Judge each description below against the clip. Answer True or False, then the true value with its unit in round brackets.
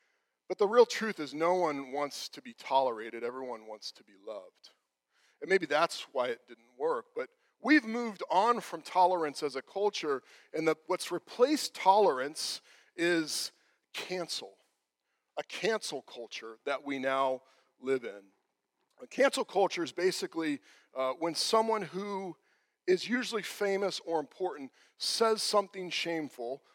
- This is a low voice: False (185 Hz)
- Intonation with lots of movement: True (8.6 semitones)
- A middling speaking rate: True (145 wpm)